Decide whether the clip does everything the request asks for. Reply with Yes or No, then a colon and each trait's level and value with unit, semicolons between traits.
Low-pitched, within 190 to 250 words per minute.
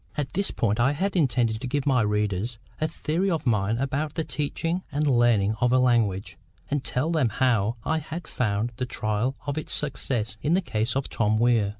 Yes: low, 125 Hz; fast, 205 wpm